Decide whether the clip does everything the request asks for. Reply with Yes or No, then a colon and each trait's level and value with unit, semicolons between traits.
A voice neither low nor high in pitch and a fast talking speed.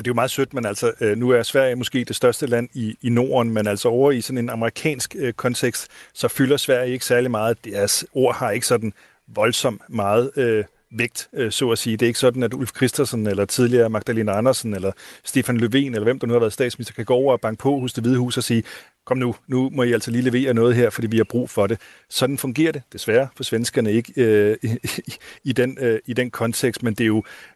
No: low, 120 Hz; fast, 250 wpm